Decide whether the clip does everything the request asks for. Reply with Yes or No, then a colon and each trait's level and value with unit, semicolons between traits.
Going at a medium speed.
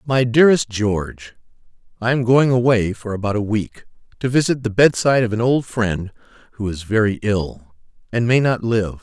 Yes: average, 175 wpm